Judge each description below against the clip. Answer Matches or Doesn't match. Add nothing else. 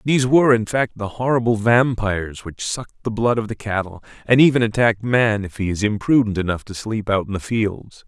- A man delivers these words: Matches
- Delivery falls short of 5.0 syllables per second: Doesn't match